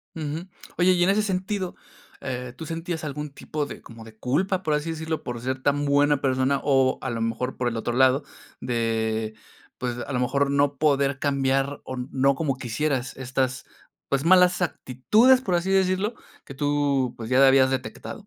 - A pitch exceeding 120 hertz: Yes, medium, 140 Hz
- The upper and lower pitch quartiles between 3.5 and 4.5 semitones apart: Yes, average, 3.8 semitones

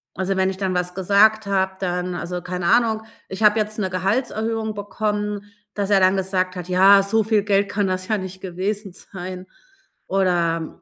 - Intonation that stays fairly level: Yes, narrow, 2.1 semitones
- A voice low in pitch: No, high, 195 Hz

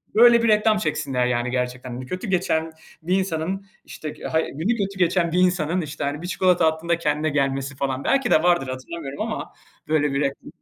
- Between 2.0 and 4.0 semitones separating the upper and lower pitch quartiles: No, average, 4.9 semitones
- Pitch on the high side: No, medium, 160 Hz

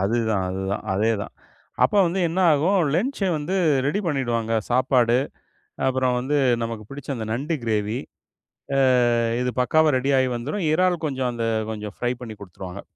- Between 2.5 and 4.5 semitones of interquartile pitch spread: No, average, 5.0 semitones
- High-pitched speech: No, low, 125 Hz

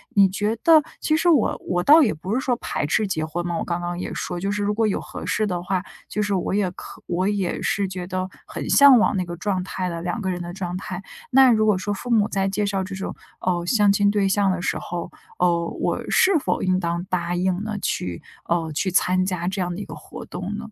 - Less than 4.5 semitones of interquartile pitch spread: Yes, average, 2.8 semitones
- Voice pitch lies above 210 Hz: No, high, 190 Hz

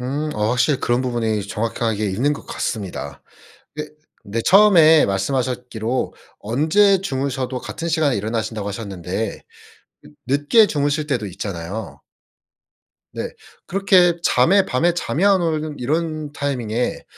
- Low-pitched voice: Yes, low, 130 Hz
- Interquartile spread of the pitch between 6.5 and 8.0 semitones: No, wide, 6.0 semitones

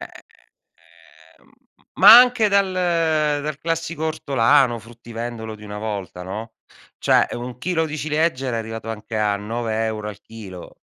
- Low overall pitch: Yes, low, 120 Hz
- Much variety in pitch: Yes, wide, 6.6 semitones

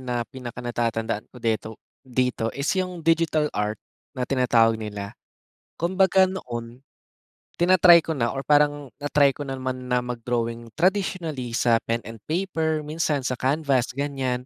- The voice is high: No, low, 130 Hz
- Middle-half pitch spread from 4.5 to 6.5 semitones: Yes, average, 4.9 semitones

